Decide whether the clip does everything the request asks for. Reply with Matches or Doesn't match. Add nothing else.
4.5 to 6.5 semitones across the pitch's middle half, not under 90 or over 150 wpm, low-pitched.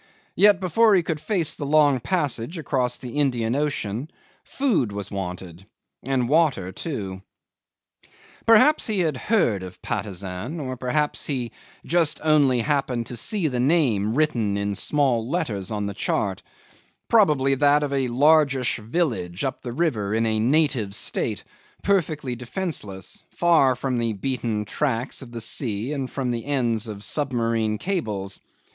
Matches